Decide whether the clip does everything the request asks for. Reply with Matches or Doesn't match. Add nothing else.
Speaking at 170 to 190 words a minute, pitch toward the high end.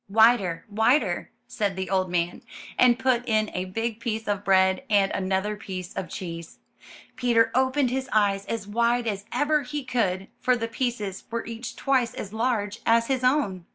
Matches